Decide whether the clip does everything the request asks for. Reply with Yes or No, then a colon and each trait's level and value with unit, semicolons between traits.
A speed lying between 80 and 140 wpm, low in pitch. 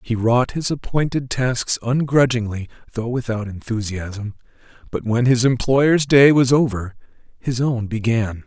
Yes: slow, 135 wpm; low, 120 Hz